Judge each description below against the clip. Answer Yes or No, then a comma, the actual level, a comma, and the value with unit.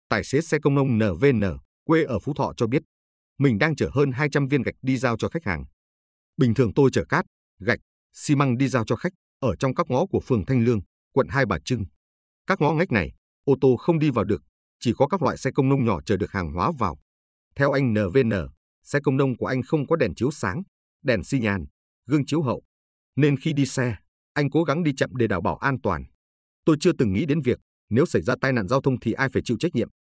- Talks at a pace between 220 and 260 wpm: Yes, average, 245 wpm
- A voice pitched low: Yes, low, 125 Hz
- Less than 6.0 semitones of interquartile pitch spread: No, wide, 8.1 semitones